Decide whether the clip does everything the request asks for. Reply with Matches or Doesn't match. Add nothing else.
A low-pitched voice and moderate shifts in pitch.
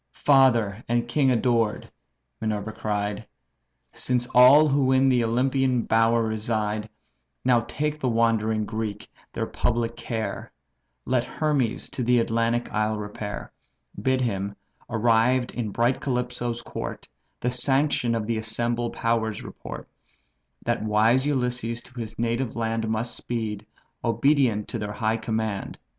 Doesn't match